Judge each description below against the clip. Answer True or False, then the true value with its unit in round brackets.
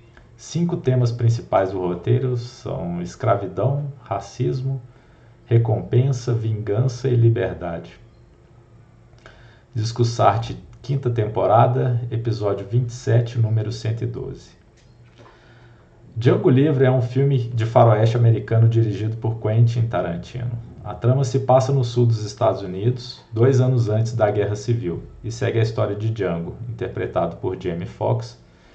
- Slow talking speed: True (115 wpm)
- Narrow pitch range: True (2.2 semitones)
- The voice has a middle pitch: False (115 Hz)